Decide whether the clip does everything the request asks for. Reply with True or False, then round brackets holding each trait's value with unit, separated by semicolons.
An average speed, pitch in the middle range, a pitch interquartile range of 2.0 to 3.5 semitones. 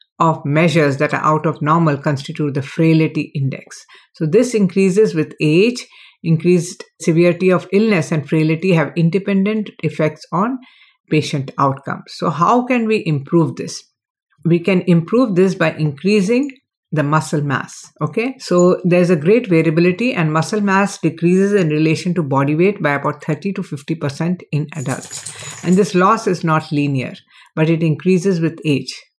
False (160 wpm; 165 Hz; 4.1 semitones)